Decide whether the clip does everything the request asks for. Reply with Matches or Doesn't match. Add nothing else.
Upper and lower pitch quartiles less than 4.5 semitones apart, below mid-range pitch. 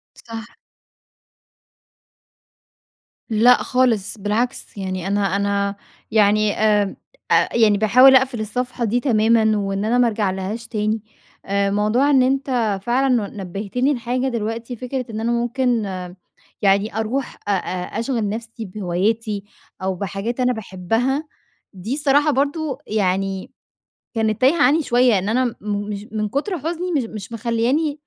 Doesn't match